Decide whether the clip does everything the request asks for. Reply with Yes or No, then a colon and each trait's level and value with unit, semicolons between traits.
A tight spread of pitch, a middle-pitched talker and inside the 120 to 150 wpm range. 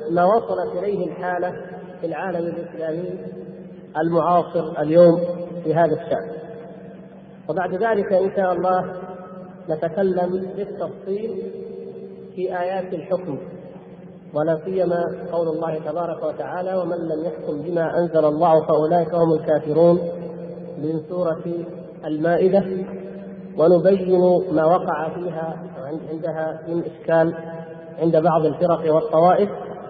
No: narrow, 1.9 semitones; medium, 170 Hz; average, 100 wpm